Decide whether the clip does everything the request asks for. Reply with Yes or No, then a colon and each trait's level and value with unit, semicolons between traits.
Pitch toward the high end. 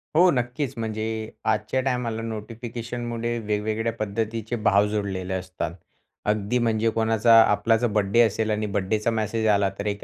No: low, 110 Hz